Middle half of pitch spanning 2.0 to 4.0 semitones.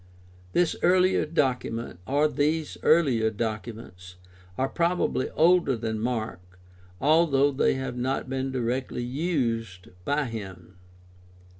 No: average, 5.2 semitones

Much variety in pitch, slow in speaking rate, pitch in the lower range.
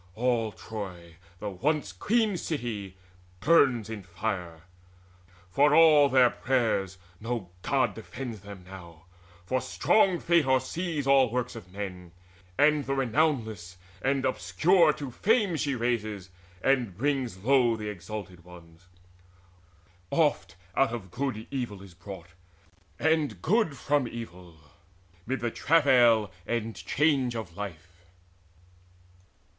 Yes: wide, 6.4 semitones; slow, 120 wpm; low, 120 Hz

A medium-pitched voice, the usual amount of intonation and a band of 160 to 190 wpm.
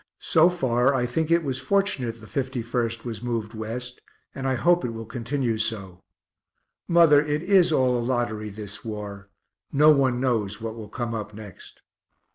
No: low, 120 Hz; average, 4.0 semitones; average, 170 wpm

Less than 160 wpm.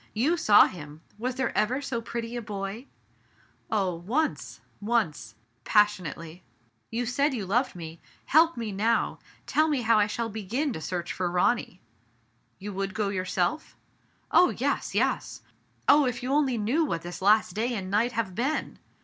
No: average, 175 wpm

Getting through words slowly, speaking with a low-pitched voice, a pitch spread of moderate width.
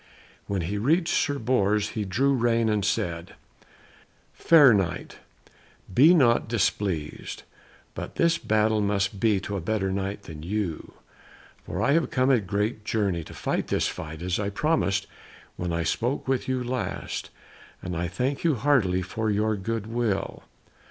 No: average, 155 wpm; low, 105 Hz; average, 4.3 semitones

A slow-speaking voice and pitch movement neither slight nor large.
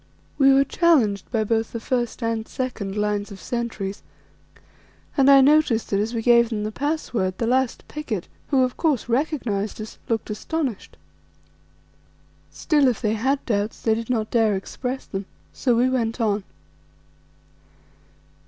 No: average, 155 wpm; average, 3.6 semitones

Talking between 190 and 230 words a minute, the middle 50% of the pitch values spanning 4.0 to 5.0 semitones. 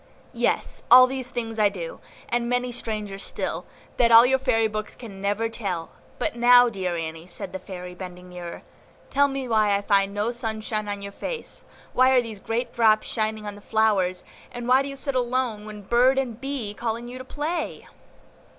No: average, 195 wpm; average, 3.6 semitones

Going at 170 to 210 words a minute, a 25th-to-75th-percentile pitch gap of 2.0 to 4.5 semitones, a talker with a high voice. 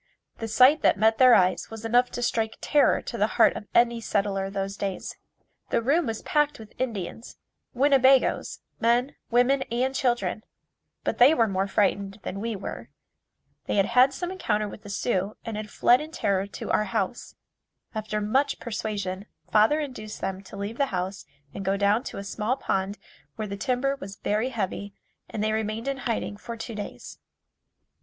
Yes: average, 185 wpm; average, 3.7 semitones; high, 220 Hz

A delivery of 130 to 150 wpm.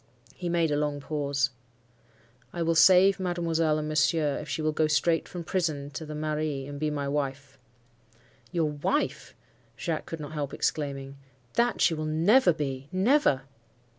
No: average, 160 wpm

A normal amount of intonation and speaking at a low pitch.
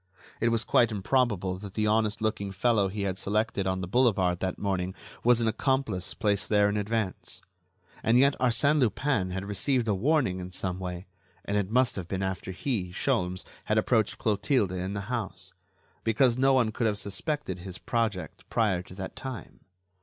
Yes: average, 3.9 semitones; low, 105 Hz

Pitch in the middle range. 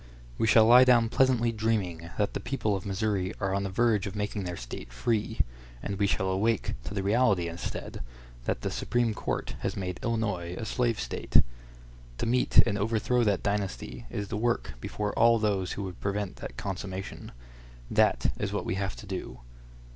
No: low, 100 Hz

